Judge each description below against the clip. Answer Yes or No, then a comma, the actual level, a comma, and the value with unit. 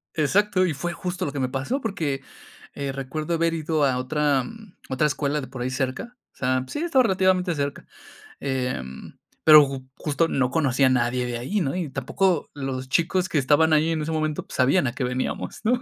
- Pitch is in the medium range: Yes, medium, 145 Hz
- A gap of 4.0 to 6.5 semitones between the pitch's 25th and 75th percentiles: Yes, average, 4.5 semitones